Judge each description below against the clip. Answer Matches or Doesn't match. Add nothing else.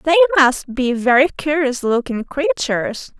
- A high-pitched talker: Matches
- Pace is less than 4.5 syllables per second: Matches